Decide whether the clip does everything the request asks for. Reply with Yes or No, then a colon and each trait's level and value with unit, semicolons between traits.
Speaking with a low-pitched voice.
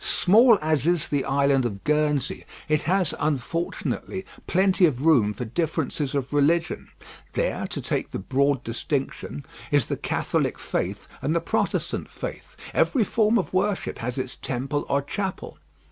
No: medium, 150 Hz